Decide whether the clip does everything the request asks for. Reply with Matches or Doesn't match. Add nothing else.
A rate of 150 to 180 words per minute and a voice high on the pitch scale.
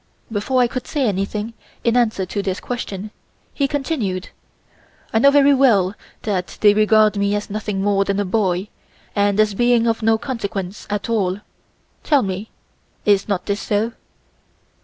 Matches